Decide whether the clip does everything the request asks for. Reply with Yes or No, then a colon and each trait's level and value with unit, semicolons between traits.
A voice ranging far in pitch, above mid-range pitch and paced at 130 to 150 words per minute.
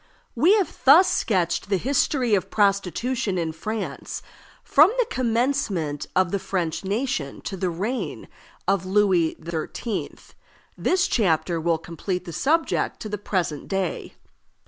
Yes: wide, 6.3 semitones; high, 195 Hz; slow, 135 wpm